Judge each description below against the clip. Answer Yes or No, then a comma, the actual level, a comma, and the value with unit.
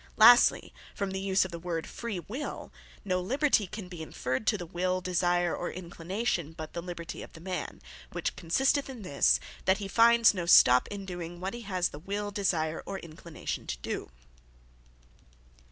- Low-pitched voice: No, medium, 185 Hz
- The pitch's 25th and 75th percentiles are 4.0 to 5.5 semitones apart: No, average, 3.2 semitones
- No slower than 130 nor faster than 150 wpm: No, average, 175 wpm